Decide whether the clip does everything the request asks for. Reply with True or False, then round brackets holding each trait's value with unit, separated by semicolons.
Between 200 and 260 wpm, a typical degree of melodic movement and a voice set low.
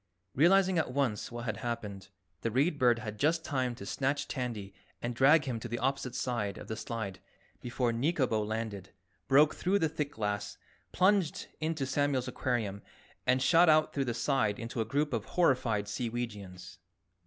False (170 wpm; 4.7 semitones; 125 Hz)